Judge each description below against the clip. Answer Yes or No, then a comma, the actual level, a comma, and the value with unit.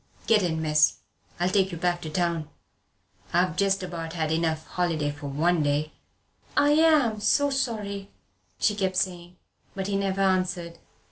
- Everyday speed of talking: Yes, average, 160 wpm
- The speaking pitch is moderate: Yes, medium, 180 Hz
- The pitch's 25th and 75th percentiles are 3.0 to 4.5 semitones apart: Yes, average, 3.6 semitones